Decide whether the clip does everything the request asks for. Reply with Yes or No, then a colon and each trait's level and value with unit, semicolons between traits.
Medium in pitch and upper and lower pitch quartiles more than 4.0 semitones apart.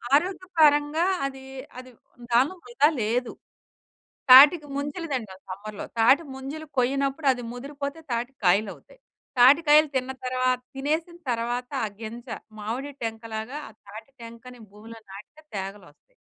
No: very high, 255 Hz; average, 4.4 semitones